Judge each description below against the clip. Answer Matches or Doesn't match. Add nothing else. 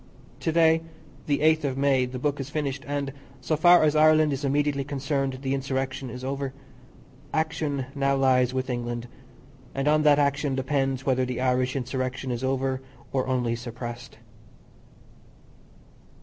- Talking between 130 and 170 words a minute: Matches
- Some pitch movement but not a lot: Doesn't match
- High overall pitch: Doesn't match